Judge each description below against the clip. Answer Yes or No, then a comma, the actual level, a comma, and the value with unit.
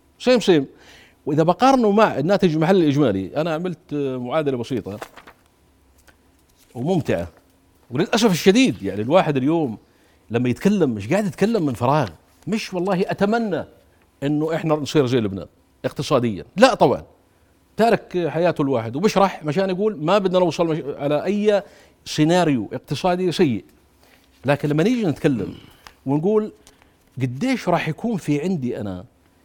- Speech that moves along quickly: No, average, 125 wpm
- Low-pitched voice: No, medium, 150 Hz